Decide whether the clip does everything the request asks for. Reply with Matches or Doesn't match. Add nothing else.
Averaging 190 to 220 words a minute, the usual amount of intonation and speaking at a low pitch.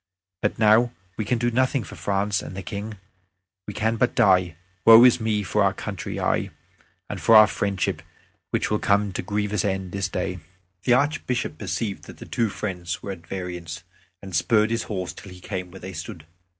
Matches